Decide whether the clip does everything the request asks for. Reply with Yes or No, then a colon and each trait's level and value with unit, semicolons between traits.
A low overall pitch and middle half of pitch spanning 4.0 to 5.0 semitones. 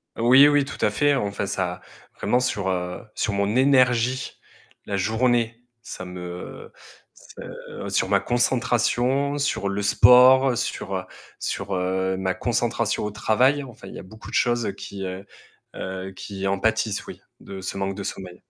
Yes: low, 105 Hz; average, 4.6 semitones